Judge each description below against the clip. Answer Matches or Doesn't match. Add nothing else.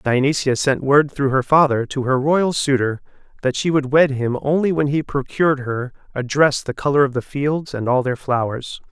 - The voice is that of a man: Matches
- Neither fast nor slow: Doesn't match